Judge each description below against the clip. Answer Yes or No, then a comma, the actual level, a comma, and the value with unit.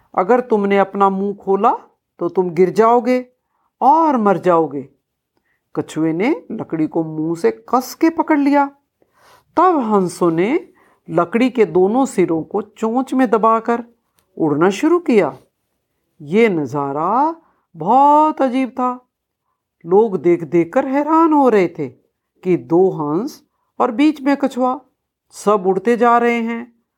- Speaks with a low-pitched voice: No, high, 225 Hz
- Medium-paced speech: Yes, average, 135 wpm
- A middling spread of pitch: No, wide, 6.8 semitones